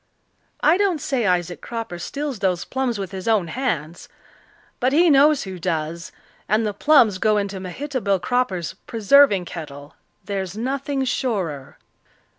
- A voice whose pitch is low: No, high, 210 Hz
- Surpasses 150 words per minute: No, average, 140 wpm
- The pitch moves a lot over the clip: Yes, wide, 6.8 semitones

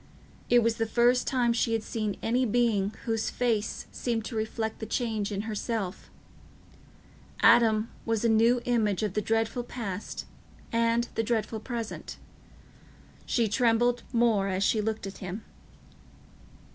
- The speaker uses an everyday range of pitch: No, narrow, 1.8 semitones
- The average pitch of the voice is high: Yes, high, 225 Hz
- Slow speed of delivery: No, average, 145 wpm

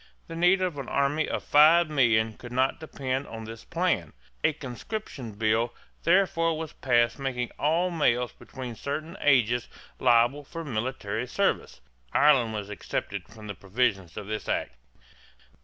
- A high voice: No, low, 130 Hz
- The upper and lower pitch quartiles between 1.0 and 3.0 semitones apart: No, wide, 5.4 semitones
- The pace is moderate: Yes, average, 150 wpm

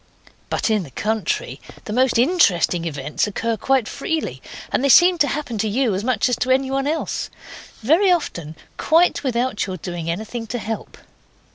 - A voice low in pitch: No, high, 235 Hz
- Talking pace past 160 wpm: Yes, average, 170 wpm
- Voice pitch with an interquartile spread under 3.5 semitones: No, average, 5.2 semitones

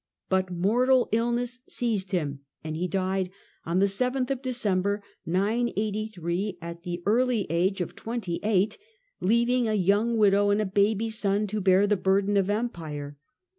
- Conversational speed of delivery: Yes, average, 145 wpm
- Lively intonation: No, average, 3.5 semitones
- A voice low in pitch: No, high, 200 Hz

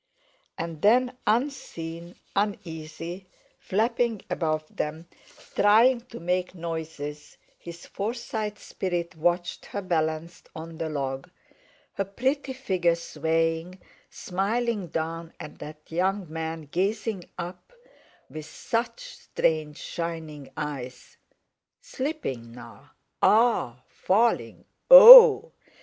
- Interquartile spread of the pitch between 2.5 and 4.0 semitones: No, average, 5.0 semitones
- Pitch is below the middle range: No, medium, 175 Hz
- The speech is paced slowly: Yes, slow, 95 wpm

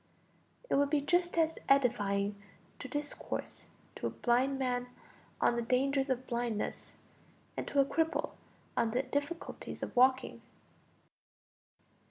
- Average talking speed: No, slow, 130 wpm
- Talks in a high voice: Yes, very high, 265 Hz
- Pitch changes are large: No, average, 2.8 semitones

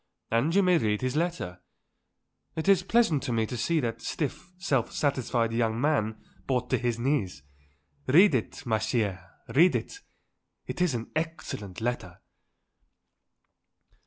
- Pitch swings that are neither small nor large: No, wide, 6.2 semitones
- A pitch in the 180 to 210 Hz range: No, low, 125 Hz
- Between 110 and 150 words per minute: Yes, average, 145 wpm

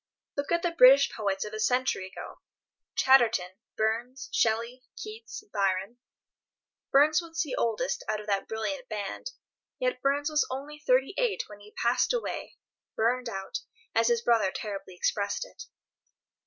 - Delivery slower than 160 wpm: Yes, average, 145 wpm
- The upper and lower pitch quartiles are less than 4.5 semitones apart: No, average, 5.2 semitones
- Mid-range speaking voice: No, high, 245 Hz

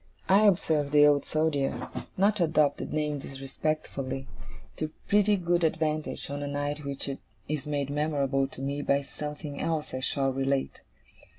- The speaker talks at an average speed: Yes, average, 160 wpm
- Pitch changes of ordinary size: No, narrow, 2.1 semitones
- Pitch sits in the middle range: Yes, medium, 145 Hz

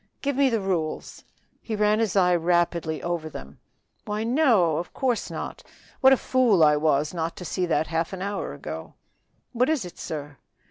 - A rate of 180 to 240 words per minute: Yes, average, 185 wpm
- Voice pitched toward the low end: No, medium, 180 Hz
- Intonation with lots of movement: Yes, wide, 5.8 semitones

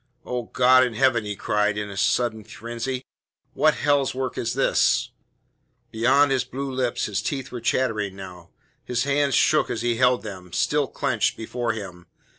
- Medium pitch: No, low, 120 Hz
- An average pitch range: Yes, average, 3.6 semitones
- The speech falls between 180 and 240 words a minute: No, average, 170 wpm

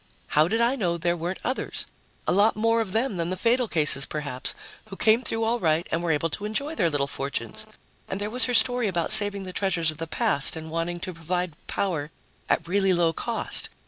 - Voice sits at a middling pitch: Yes, medium, 180 Hz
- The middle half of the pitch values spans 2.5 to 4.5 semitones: No, average, 5.1 semitones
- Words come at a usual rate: No, fast, 220 wpm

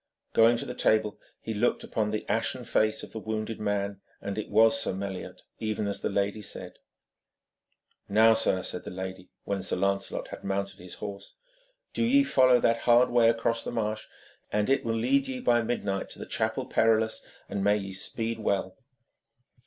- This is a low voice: Yes, low, 110 Hz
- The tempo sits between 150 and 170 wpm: No, average, 185 wpm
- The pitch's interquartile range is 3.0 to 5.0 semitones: No, narrow, 2.6 semitones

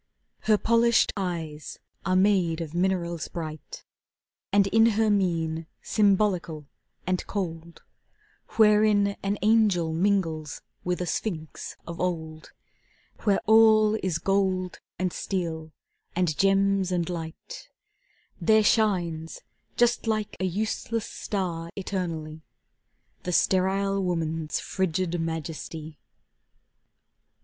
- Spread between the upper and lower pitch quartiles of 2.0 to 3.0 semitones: No, average, 3.7 semitones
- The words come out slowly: Yes, slow, 105 wpm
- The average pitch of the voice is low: No, medium, 185 Hz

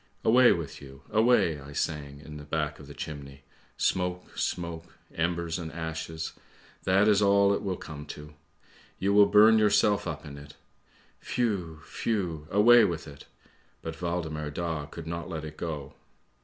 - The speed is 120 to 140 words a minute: No, average, 165 wpm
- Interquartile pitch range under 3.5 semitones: No, average, 4.7 semitones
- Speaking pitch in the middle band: No, very low, 80 Hz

